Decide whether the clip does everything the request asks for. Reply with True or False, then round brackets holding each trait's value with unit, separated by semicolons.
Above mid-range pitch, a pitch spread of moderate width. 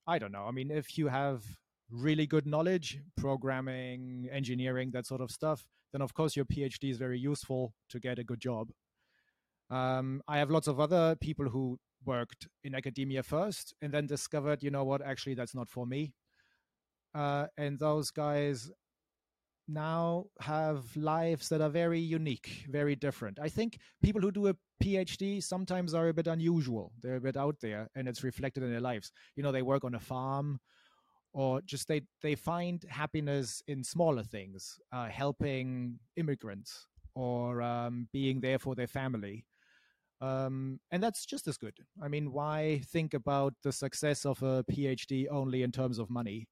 False (135 Hz; 3.3 semitones)